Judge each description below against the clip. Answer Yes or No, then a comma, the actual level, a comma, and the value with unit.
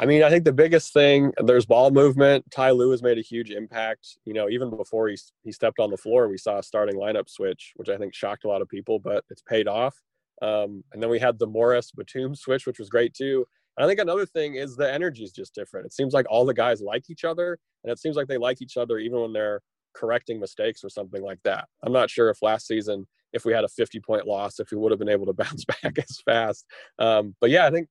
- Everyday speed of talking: No, fast, 265 wpm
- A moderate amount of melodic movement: No, wide, 6.1 semitones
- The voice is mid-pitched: No, low, 130 Hz